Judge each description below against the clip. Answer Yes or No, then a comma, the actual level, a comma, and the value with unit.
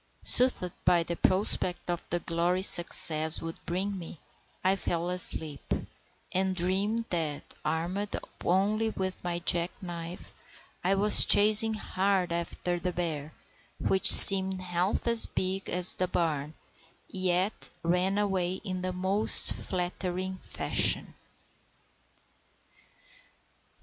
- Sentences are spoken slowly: Yes, slow, 115 wpm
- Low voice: No, medium, 180 Hz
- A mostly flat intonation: Yes, narrow, 1.9 semitones